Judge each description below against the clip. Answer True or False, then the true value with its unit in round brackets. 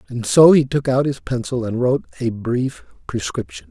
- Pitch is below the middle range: True (125 Hz)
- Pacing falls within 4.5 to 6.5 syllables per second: True (5.1 syllables/s)